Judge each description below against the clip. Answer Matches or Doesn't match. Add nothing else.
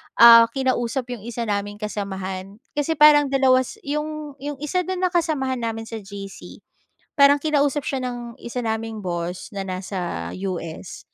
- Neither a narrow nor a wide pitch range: Doesn't match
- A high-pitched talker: Matches